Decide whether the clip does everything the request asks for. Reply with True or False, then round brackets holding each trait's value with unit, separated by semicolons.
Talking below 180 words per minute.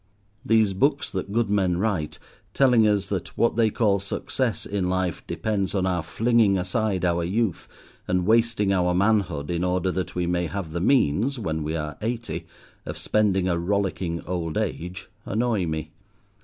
True (170 wpm)